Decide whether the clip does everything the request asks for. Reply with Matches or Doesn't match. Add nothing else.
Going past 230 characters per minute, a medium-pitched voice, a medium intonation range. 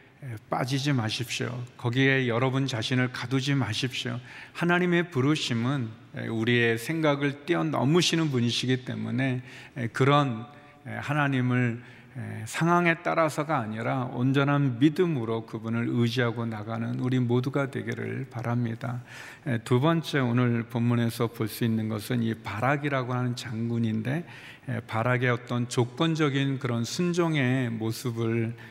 Doesn't match